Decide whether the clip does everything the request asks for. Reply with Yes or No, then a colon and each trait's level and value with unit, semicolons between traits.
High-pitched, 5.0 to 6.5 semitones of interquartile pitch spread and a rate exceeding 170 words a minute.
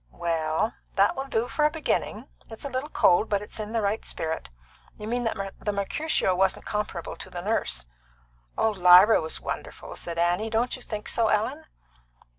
No: high, 210 Hz; average, 4.3 semitones; average, 185 wpm